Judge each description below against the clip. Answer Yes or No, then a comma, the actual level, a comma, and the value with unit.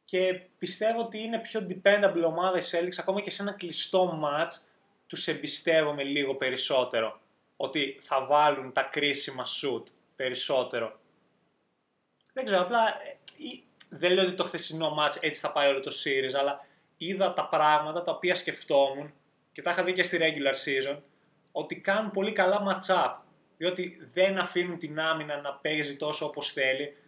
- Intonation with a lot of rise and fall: No, average, 4.2 semitones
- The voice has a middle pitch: Yes, medium, 165 Hz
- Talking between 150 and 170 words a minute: Yes, average, 160 wpm